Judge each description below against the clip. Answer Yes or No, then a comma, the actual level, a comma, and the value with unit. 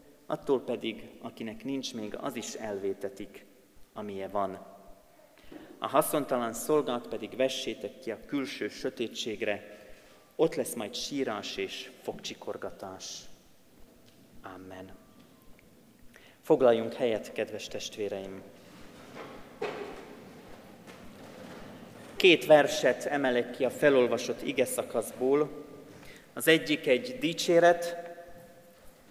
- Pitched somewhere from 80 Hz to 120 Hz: No, low, 130 Hz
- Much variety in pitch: Yes, wide, 7.2 semitones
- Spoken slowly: Yes, slow, 85 wpm